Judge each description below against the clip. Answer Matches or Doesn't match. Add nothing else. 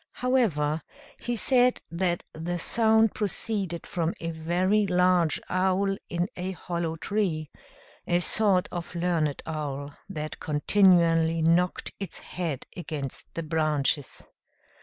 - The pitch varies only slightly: Doesn't match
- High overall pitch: Doesn't match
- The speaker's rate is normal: Doesn't match